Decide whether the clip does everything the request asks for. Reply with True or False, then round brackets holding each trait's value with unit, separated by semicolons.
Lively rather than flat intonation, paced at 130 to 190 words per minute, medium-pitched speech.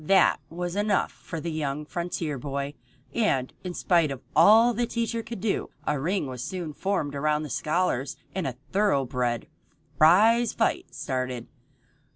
True (6.0 semitones; 155 wpm; 165 Hz)